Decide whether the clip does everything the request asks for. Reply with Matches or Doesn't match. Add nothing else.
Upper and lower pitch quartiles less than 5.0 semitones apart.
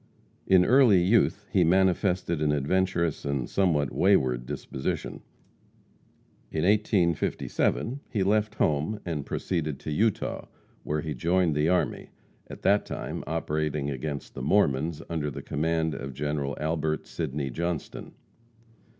Matches